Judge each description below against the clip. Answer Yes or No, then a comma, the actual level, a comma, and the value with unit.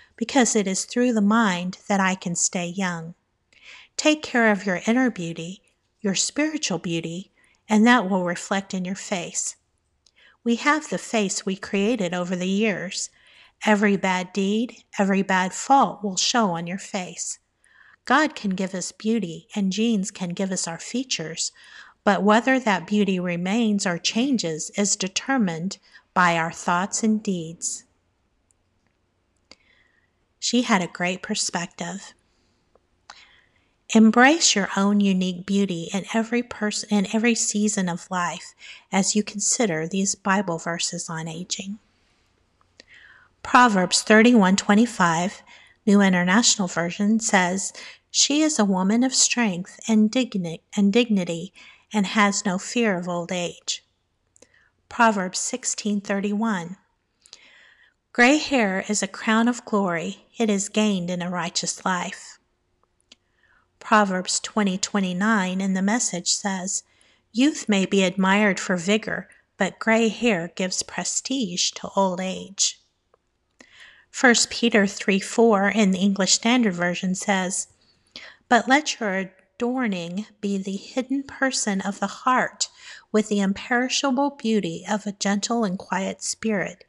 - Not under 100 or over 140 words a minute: Yes, slow, 135 wpm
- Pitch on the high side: Yes, high, 200 Hz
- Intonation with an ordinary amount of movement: Yes, average, 3.5 semitones